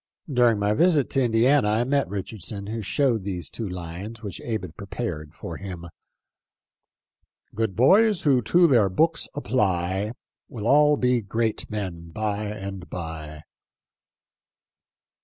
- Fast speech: No, average, 140 wpm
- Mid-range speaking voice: No, low, 105 Hz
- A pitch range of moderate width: Yes, average, 4.9 semitones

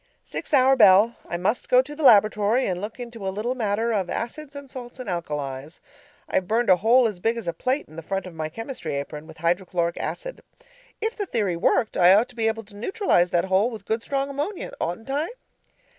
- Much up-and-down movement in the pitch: Yes, wide, 6.0 semitones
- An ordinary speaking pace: No, fast, 220 wpm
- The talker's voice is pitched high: Yes, high, 220 Hz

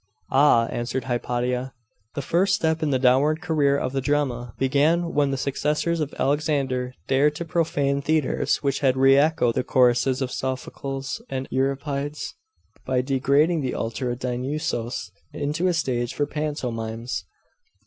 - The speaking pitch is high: No, low, 135 Hz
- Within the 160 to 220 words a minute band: No, average, 150 wpm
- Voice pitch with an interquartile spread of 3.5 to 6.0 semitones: No, average, 2.8 semitones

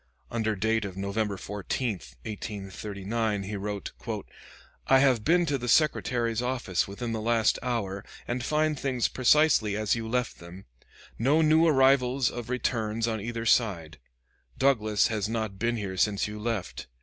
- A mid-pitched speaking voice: No, low, 115 Hz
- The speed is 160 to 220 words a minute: No, average, 150 wpm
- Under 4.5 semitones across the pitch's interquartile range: Yes, average, 3.5 semitones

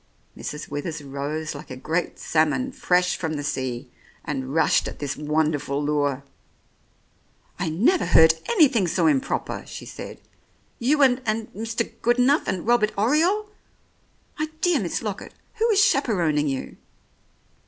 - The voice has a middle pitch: Yes, medium, 180 Hz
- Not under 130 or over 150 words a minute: Yes, average, 145 wpm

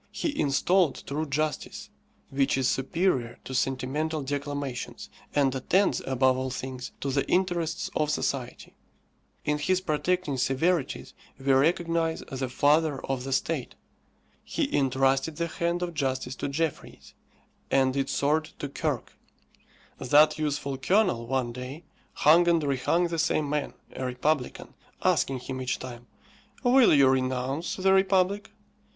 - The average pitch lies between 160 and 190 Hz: No, medium, 145 Hz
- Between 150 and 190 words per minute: No, slow, 135 wpm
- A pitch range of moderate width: Yes, average, 3.8 semitones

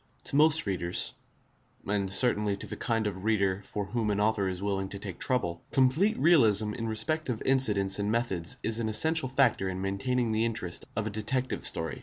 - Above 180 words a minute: Yes, average, 195 wpm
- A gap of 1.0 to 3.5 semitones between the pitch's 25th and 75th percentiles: No, average, 4.3 semitones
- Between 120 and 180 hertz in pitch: No, low, 110 Hz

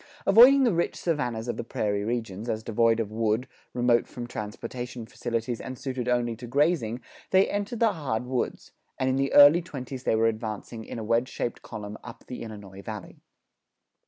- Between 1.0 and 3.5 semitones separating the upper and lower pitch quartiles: Yes, average, 2.9 semitones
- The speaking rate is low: No, average, 185 wpm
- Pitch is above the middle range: No, low, 120 Hz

